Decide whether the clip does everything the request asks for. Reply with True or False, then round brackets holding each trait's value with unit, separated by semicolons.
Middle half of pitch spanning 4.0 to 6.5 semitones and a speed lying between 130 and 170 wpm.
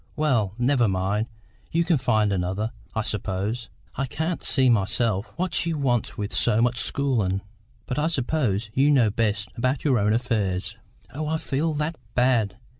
True (5.2 semitones; 165 wpm)